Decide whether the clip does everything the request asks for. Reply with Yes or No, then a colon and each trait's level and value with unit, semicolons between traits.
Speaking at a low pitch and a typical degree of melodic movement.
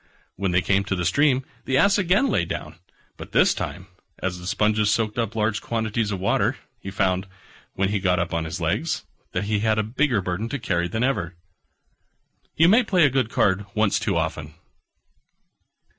Yes: low, 105 Hz; average, 4.4 semitones